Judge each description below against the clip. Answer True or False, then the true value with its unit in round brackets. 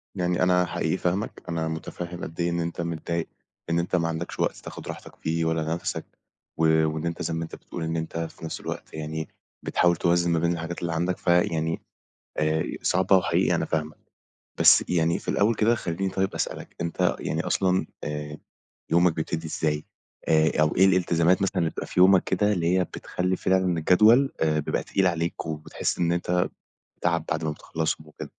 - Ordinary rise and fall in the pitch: False (1.9 semitones)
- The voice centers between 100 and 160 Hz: False (85 Hz)